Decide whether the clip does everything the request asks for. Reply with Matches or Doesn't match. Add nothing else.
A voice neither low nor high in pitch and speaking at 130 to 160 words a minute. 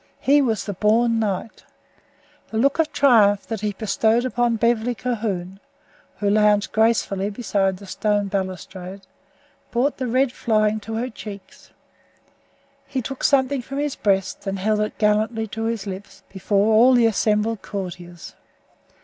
Doesn't match